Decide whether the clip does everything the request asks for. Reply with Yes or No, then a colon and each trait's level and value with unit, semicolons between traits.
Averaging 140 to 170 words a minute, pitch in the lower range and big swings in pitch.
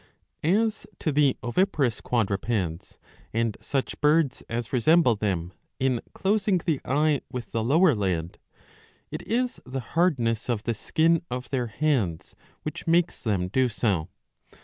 Yes: average, 145 wpm; low, 125 Hz; wide, 6.1 semitones